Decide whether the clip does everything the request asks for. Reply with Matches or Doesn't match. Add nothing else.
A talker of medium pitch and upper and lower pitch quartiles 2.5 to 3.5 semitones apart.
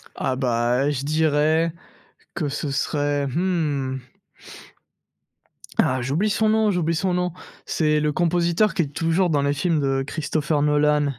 Matches